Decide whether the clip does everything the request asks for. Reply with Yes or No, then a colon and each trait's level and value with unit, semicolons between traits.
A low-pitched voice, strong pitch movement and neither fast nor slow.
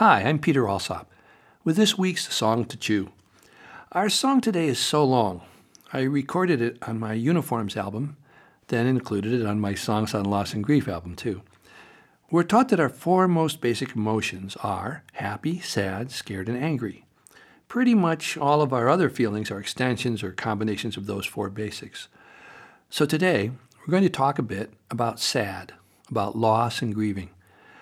Yes: low, 120 Hz; wide, 6.6 semitones; average, 170 wpm